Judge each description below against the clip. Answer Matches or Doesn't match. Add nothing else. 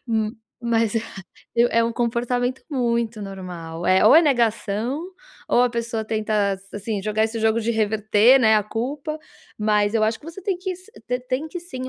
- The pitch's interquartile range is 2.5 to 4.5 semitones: Matches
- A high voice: Matches